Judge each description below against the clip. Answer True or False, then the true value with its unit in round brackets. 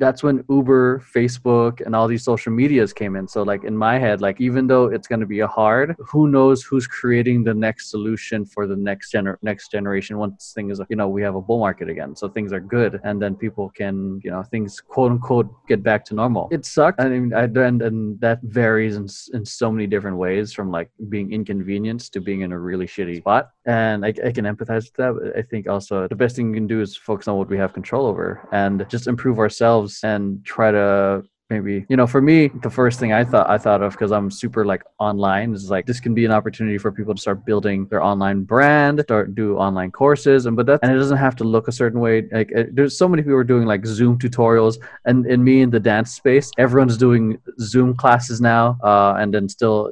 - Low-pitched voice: True (110 Hz)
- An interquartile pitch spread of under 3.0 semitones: False (3.3 semitones)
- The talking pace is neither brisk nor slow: False (235 wpm)